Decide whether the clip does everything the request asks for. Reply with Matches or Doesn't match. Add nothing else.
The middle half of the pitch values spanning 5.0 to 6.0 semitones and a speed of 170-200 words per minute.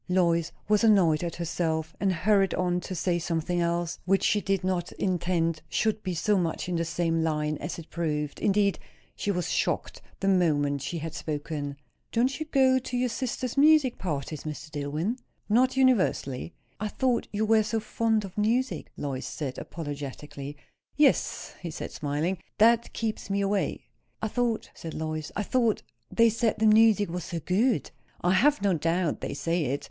Matches